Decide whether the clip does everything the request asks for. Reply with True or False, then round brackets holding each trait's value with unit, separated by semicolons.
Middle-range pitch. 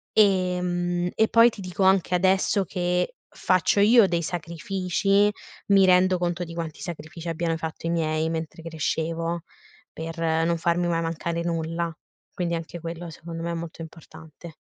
True (170 Hz)